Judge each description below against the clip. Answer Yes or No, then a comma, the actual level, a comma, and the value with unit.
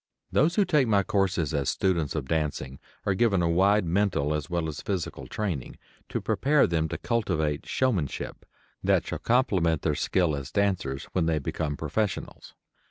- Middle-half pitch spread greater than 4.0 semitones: Yes, average, 4.9 semitones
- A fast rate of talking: No, average, 165 wpm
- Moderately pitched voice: No, very low, 85 Hz